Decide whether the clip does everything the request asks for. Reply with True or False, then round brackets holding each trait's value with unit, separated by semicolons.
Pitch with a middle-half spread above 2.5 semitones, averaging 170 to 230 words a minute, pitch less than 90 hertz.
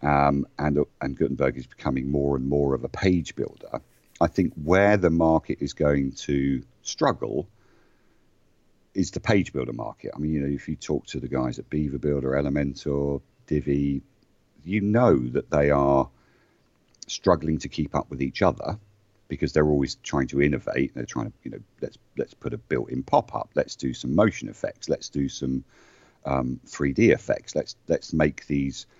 False (2.2 semitones; 180 wpm; 70 Hz)